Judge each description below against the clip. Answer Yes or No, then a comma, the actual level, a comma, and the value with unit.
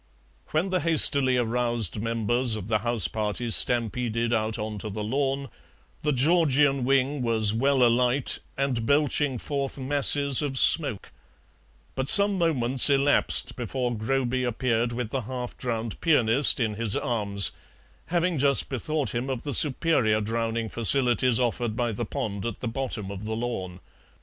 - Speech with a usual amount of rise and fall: Yes, average, 3.5 semitones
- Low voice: Yes, low, 125 Hz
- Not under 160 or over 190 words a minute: No, average, 150 wpm